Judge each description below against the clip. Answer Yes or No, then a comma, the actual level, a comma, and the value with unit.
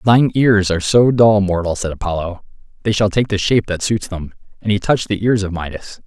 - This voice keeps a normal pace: No, fast, 240 wpm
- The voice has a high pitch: No, low, 100 Hz